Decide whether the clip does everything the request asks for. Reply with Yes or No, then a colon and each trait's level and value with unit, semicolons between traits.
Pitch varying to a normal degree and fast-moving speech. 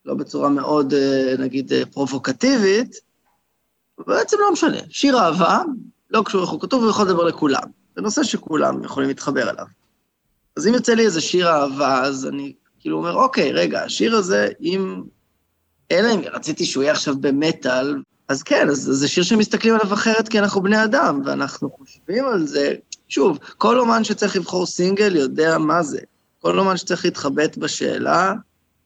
No: wide, 8.1 semitones; fast, 160 wpm